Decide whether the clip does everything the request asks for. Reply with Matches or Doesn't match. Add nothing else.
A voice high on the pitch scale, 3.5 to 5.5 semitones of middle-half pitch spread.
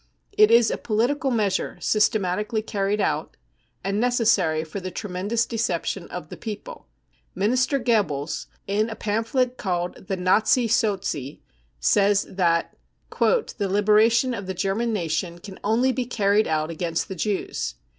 Matches